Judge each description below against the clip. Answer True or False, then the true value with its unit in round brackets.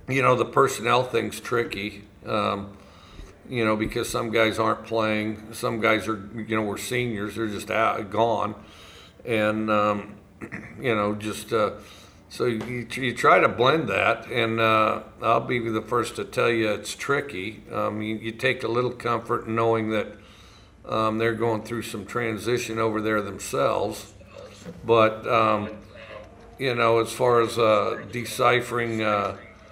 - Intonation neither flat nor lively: False (1.7 semitones)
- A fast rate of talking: False (155 wpm)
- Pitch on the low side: True (110 Hz)